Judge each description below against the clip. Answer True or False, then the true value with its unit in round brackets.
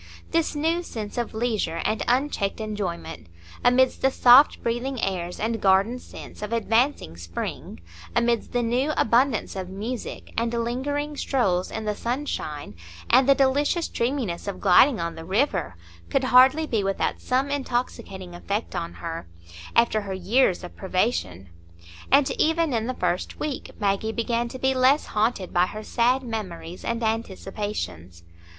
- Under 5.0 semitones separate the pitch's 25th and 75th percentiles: False (5.3 semitones)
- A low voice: False (230 Hz)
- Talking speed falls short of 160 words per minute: True (145 wpm)